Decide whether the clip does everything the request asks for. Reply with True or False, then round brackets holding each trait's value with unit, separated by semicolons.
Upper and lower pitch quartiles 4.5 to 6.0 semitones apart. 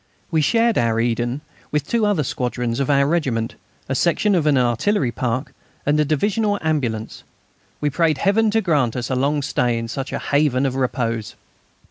True (4.8 semitones)